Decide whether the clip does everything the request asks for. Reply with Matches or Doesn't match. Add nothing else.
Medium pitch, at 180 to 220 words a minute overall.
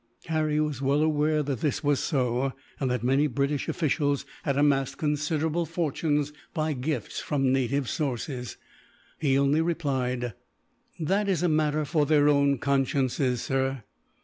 Doesn't match